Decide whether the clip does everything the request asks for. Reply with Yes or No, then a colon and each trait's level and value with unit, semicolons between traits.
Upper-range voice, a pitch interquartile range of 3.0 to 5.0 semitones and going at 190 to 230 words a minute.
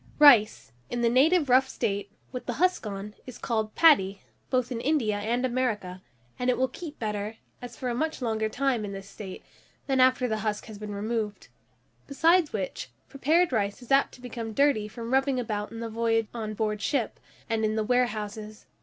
Yes: high, 230 Hz; average, 3.5 semitones; average, 195 wpm